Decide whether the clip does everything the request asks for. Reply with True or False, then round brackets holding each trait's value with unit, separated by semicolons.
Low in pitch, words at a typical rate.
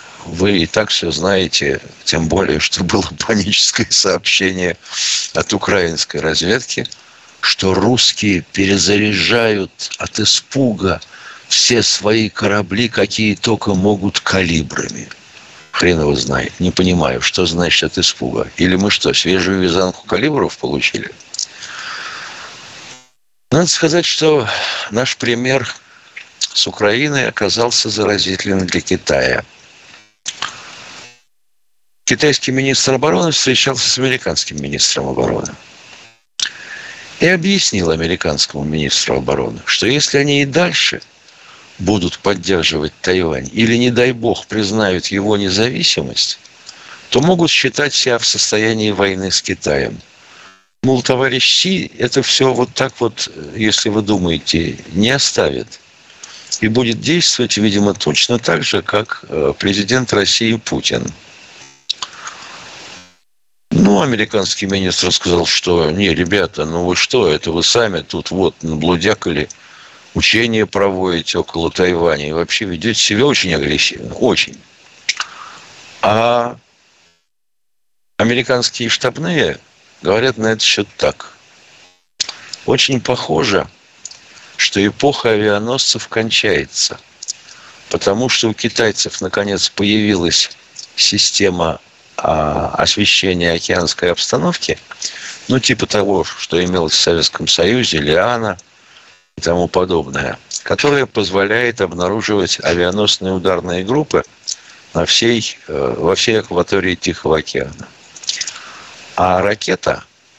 False (105 Hz; 105 wpm)